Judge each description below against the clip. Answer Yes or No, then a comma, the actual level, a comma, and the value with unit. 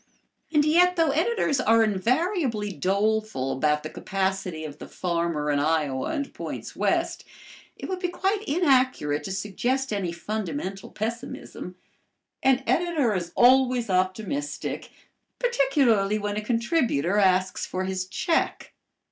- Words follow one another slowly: Yes, slow, 130 wpm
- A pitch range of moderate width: No, wide, 7.0 semitones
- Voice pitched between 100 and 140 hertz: No, high, 215 Hz